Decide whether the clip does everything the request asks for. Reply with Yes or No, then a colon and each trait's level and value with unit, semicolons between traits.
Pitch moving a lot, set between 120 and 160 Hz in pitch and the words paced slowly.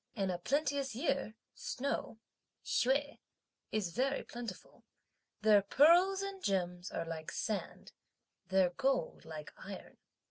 No: wide, 7.2 semitones; high, 225 Hz; slow, 115 wpm